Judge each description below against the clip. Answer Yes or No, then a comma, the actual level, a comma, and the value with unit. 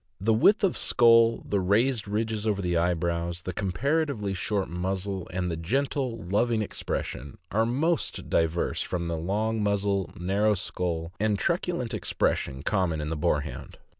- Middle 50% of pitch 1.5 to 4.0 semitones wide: No, average, 4.5 semitones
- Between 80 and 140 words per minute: No, average, 150 wpm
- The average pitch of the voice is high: No, low, 100 Hz